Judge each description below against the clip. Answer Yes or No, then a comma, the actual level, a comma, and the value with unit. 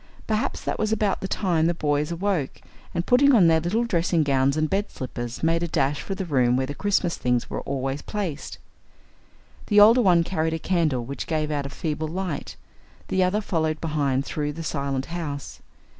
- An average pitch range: Yes, average, 4.9 semitones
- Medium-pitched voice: Yes, medium, 160 Hz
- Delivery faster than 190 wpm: Yes, average, 200 wpm